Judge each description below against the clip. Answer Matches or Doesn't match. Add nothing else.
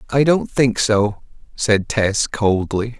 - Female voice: Doesn't match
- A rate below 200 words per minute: Matches